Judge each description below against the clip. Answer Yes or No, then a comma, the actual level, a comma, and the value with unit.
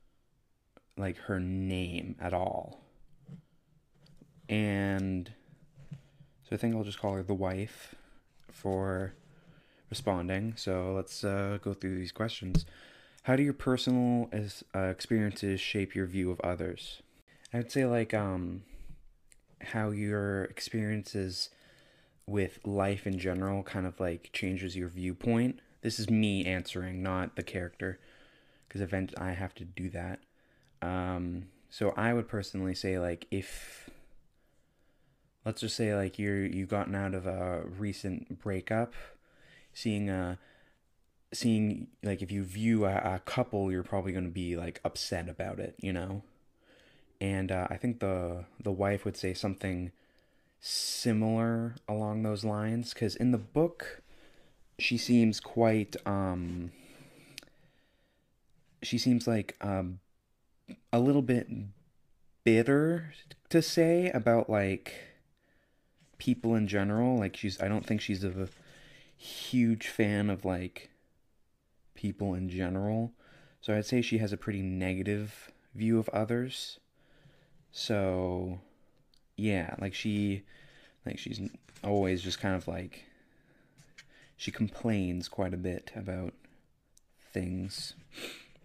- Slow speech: Yes, slow, 125 wpm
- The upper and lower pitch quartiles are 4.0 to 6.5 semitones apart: No, average, 3.6 semitones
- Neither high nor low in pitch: No, low, 100 Hz